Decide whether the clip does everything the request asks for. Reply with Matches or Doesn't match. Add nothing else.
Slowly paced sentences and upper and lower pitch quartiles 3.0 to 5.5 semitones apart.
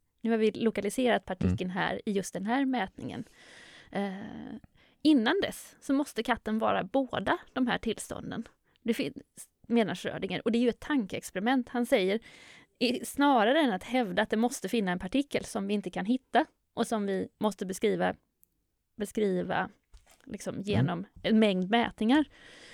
Doesn't match